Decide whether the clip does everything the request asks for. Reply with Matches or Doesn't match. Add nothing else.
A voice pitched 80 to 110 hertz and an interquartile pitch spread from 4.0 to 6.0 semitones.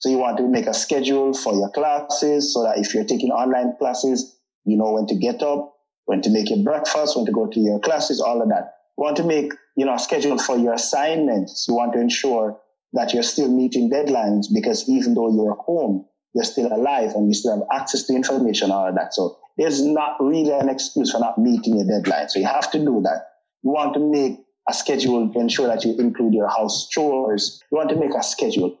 Doesn't match